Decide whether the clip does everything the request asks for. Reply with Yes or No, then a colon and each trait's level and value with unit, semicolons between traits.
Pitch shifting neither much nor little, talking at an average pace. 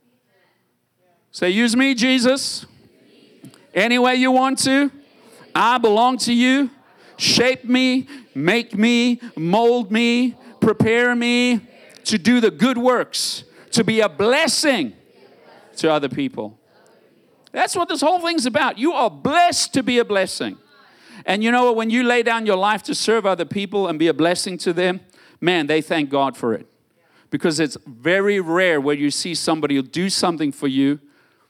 No: wide, 6.0 semitones; average, 165 wpm